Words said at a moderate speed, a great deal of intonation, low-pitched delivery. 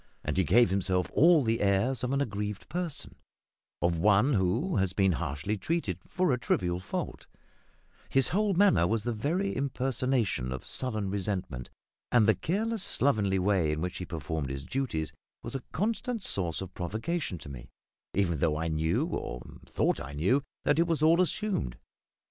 Yes: average, 170 wpm; wide, 8.3 semitones; low, 105 Hz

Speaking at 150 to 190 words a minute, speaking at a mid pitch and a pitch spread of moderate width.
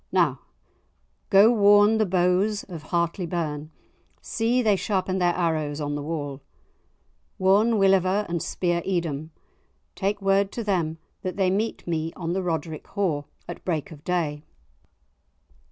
No: average, 140 wpm; medium, 180 Hz; average, 3.7 semitones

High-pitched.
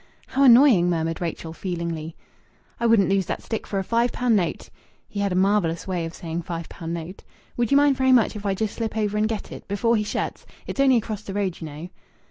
Yes: high, 200 Hz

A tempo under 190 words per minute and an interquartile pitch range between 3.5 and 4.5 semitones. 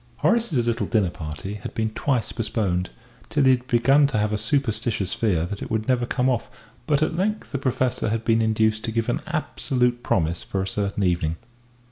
No: average, 200 wpm; average, 3.9 semitones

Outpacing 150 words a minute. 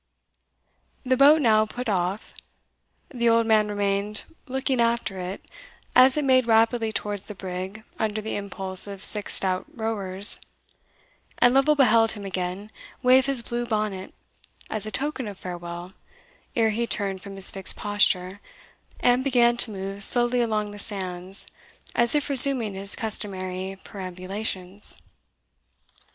No: average, 140 wpm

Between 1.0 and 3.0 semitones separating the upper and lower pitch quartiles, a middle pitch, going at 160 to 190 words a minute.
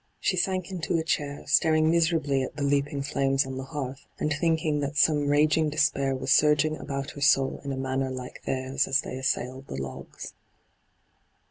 Yes: narrow, 2.5 semitones; medium, 145 Hz; average, 180 wpm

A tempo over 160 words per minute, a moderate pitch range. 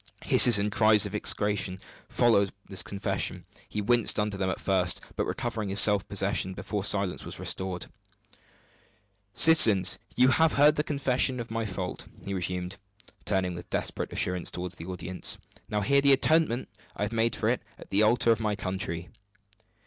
Yes: average, 170 wpm; average, 3.8 semitones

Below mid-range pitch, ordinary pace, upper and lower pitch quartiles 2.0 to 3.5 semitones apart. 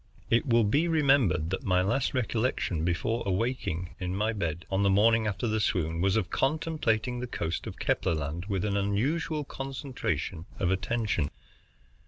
No: low, 105 Hz; average, 165 wpm; wide, 5.4 semitones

